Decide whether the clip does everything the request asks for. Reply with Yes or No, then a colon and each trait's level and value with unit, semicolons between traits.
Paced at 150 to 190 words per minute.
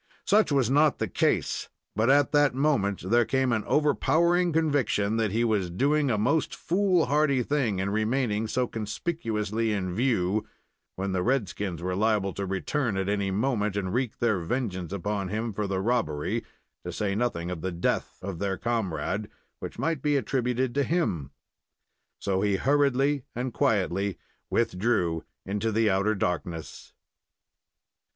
Yes: average, 155 wpm